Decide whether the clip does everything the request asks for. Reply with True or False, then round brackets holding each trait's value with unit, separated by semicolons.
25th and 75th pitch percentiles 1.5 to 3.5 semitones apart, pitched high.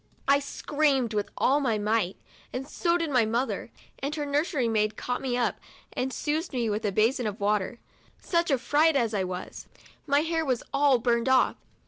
False (4.6 semitones; 255 Hz)